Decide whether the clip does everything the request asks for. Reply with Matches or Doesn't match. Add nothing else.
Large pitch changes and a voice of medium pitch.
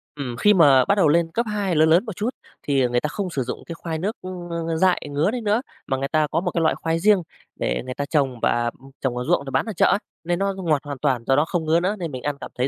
Doesn't match